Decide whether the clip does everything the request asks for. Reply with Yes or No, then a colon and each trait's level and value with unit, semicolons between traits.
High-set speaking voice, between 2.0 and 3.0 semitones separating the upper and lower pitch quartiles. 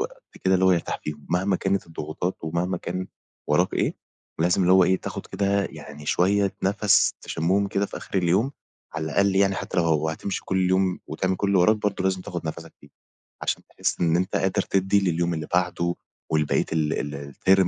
No: very low, 95 Hz; average, 2.7 semitones